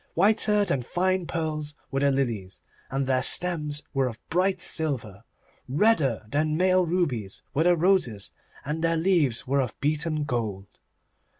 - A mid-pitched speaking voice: Yes, medium, 150 Hz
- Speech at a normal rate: Yes, average, 145 wpm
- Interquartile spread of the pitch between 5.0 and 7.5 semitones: Yes, wide, 5.4 semitones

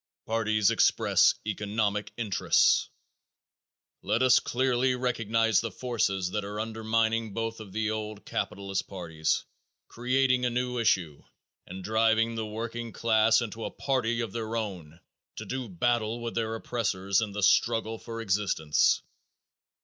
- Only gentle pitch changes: Yes, narrow, 2.2 semitones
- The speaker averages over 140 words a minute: No, slow, 135 wpm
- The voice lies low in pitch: Yes, low, 110 Hz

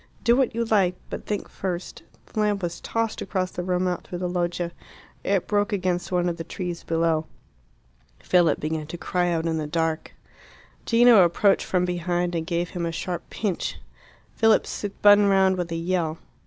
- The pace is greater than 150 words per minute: Yes, average, 185 wpm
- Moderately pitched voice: Yes, medium, 180 Hz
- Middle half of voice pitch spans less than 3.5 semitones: Yes, average, 2.7 semitones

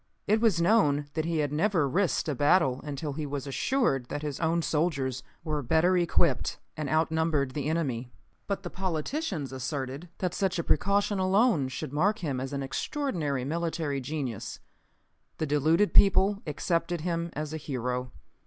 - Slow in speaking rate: No, average, 160 wpm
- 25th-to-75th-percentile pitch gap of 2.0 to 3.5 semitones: No, average, 4.2 semitones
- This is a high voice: No, medium, 155 Hz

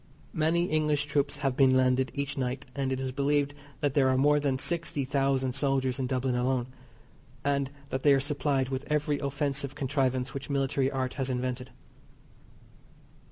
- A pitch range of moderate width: No, narrow, 1.7 semitones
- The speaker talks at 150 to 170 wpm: Yes, average, 165 wpm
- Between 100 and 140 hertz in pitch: Yes, low, 135 Hz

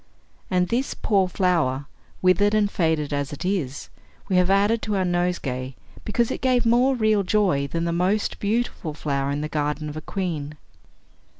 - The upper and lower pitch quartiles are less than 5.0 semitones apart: No, wide, 5.6 semitones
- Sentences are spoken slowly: No, average, 175 wpm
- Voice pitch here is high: No, medium, 180 Hz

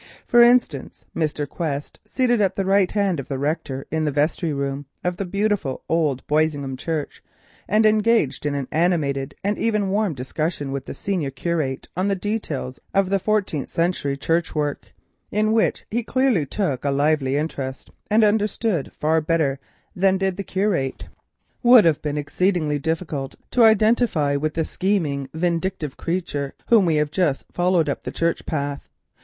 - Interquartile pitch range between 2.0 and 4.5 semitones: No, wide, 5.6 semitones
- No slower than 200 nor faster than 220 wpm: No, average, 160 wpm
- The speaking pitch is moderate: Yes, medium, 165 Hz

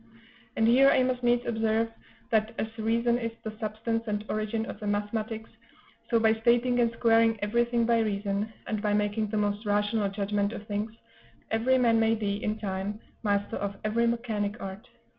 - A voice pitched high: Yes, high, 220 Hz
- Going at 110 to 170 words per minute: No, average, 180 wpm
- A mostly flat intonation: Yes, narrow, 1.8 semitones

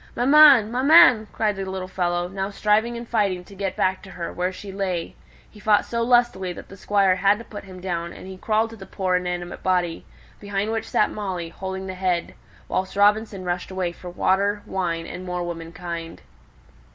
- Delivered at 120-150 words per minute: No, average, 195 wpm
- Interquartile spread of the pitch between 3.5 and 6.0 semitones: No, average, 2.8 semitones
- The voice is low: No, high, 190 Hz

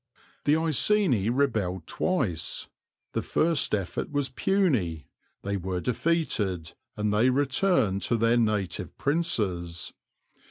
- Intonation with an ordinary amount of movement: No, wide, 7.8 semitones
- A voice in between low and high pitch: No, low, 115 Hz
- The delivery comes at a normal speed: No, slow, 110 wpm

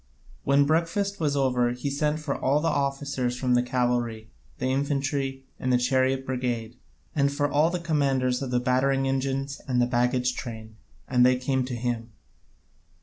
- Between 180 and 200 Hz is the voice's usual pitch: No, low, 130 Hz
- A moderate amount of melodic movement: No, narrow, 2.2 semitones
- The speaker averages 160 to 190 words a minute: Yes, average, 165 wpm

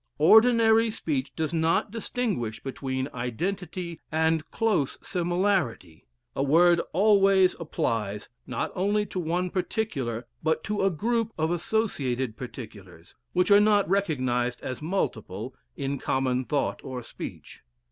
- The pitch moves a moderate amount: No, wide, 7.4 semitones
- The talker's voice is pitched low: No, medium, 160 Hz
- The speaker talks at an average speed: No, slow, 125 wpm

